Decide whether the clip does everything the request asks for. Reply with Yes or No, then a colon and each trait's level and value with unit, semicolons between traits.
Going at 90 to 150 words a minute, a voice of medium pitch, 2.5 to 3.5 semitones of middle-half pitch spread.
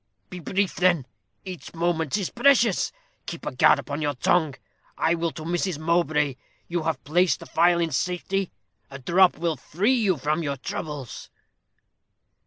No: average, 160 wpm; medium, 170 Hz; average, 3.2 semitones